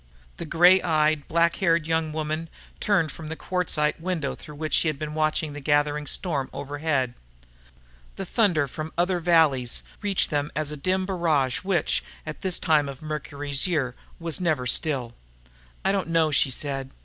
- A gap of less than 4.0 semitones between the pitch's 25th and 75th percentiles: Yes, average, 2.7 semitones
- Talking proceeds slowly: No, average, 170 wpm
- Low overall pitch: No, medium, 155 Hz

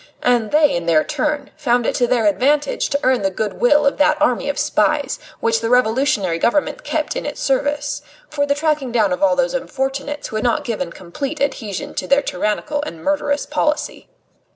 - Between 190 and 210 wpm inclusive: Yes, average, 200 wpm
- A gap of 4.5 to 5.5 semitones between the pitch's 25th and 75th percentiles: Yes, average, 4.9 semitones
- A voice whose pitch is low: No, very high, 270 Hz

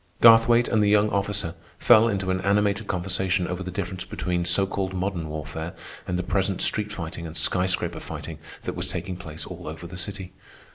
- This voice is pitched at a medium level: No, very low, 95 Hz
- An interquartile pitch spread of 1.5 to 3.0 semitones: Yes, narrow, 2.6 semitones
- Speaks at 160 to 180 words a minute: No, average, 195 wpm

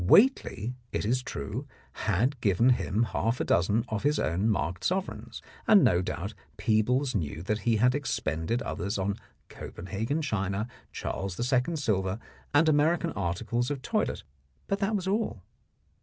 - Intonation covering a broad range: Yes, wide, 6.5 semitones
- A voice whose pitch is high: No, low, 115 Hz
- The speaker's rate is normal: Yes, average, 150 wpm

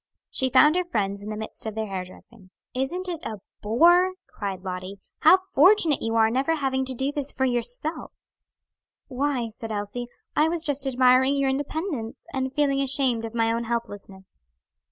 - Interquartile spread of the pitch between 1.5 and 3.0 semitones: No, average, 4.6 semitones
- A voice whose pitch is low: No, very high, 255 Hz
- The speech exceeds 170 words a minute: Yes, average, 180 wpm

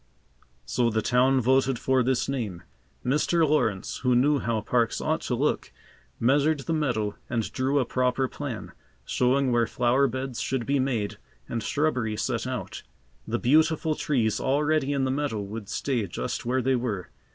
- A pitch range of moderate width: Yes, average, 3.0 semitones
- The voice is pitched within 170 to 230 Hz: No, low, 130 Hz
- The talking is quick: No, average, 165 wpm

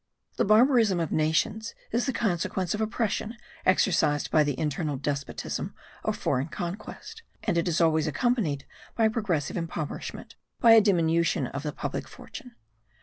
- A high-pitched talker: No, medium, 175 Hz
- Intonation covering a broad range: Yes, wide, 6.1 semitones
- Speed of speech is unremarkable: Yes, average, 145 wpm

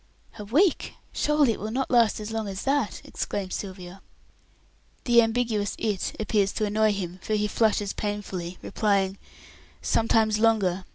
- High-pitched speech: Yes, high, 210 Hz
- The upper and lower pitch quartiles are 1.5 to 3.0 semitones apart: Yes, narrow, 2.4 semitones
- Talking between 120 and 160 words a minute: Yes, average, 150 wpm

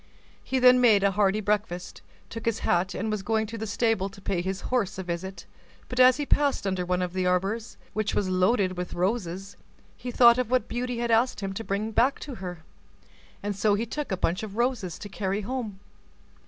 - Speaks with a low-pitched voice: No, high, 205 Hz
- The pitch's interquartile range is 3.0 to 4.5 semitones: Yes, average, 3.9 semitones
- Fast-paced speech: Yes, fast, 215 wpm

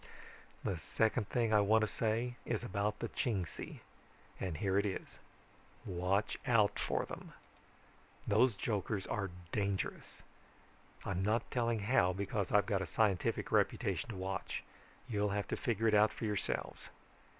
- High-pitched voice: No, low, 105 Hz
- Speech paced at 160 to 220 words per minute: No, average, 150 wpm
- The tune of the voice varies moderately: No, narrow, 2.3 semitones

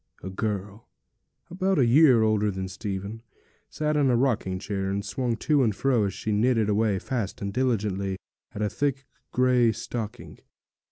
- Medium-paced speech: Yes, average, 165 wpm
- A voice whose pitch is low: Yes, low, 110 Hz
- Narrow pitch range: No, average, 4.2 semitones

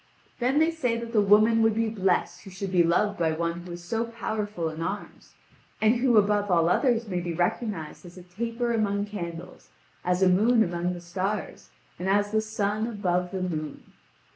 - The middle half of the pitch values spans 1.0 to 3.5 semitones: No, average, 4.0 semitones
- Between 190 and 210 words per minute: Yes, average, 195 wpm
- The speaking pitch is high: Yes, high, 200 Hz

